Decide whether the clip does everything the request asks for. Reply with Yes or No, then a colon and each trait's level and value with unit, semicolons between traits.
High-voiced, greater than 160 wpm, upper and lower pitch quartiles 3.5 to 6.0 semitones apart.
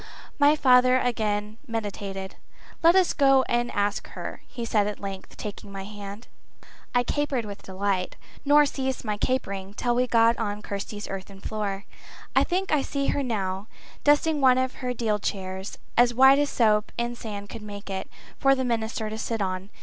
Yes: high, 220 Hz; average, 180 wpm; average, 4.2 semitones